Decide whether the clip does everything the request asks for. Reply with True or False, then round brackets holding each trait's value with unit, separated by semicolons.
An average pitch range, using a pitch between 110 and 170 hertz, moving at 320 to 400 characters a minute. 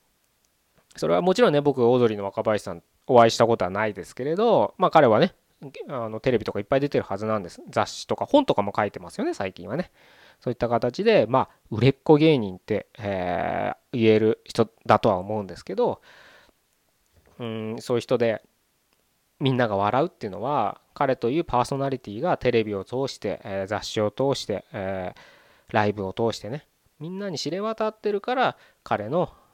True (4.8 semitones; 115 Hz; 370 characters per minute)